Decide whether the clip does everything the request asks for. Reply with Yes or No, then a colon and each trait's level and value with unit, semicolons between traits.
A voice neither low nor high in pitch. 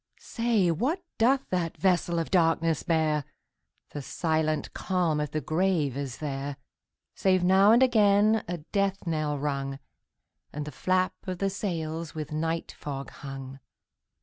Yes: medium, 165 Hz